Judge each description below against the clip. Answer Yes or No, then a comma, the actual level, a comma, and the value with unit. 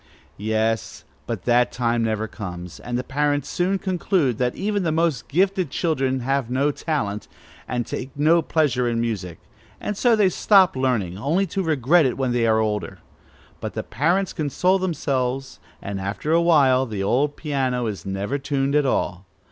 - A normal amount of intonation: No, wide, 5.8 semitones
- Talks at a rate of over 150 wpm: Yes, average, 170 wpm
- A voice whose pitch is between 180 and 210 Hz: No, low, 135 Hz